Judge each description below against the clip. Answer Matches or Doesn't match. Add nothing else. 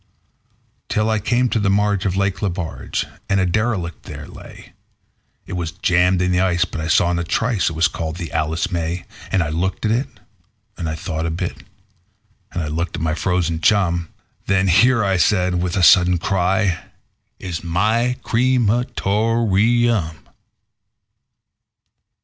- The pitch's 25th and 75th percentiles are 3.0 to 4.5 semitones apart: Matches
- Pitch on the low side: Matches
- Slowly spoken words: Doesn't match